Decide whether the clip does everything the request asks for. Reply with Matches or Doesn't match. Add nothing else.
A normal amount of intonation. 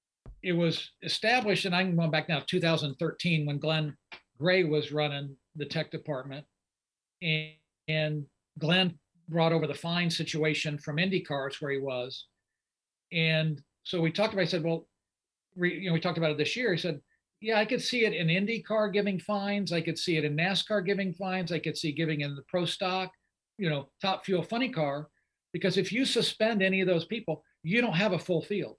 Matches